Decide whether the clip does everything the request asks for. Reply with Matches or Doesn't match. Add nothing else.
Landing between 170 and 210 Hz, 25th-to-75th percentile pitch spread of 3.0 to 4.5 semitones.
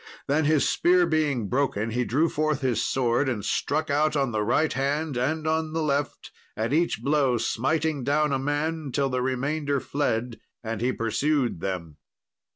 Doesn't match